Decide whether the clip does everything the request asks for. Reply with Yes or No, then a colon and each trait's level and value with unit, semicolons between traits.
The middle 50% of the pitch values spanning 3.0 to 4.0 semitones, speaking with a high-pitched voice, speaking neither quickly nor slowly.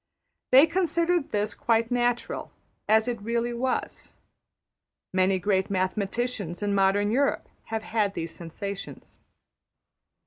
No: average, 3.7 semitones; high, 220 Hz; slow, 110 wpm